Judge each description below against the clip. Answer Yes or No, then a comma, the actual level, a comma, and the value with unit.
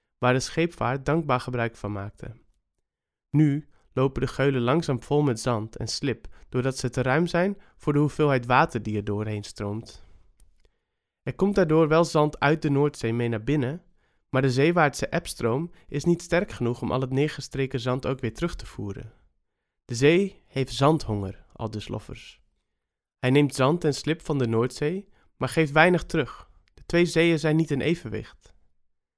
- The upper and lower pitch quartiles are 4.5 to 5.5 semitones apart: Yes, average, 5.1 semitones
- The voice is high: No, low, 135 Hz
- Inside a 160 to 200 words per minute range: Yes, average, 175 wpm